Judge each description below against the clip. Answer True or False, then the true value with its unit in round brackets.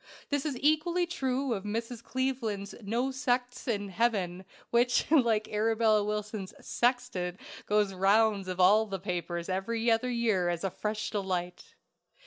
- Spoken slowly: False (145 wpm)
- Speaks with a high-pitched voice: True (215 Hz)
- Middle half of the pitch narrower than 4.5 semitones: True (4.1 semitones)